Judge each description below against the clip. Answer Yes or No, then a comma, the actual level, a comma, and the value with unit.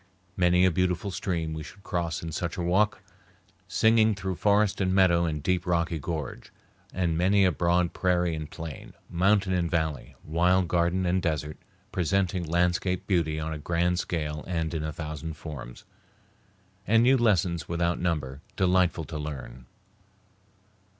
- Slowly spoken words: No, average, 155 wpm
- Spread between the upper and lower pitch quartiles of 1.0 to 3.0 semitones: Yes, narrow, 2.6 semitones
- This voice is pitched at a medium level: No, very low, 85 Hz